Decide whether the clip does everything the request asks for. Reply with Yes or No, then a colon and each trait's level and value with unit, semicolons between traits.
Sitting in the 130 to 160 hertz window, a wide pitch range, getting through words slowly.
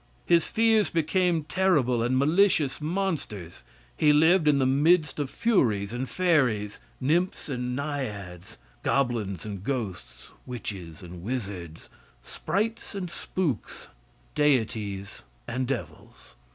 Yes: low, 135 Hz; wide, 7.8 semitones; slow, 110 wpm